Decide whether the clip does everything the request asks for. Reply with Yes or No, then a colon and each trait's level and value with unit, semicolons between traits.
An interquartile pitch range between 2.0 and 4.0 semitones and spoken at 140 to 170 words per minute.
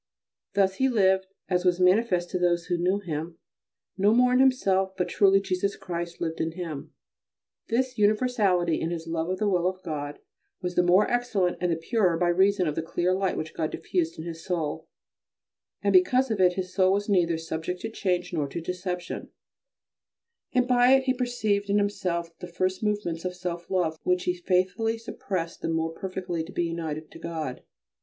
No: average, 3.1 semitones; average, 195 wpm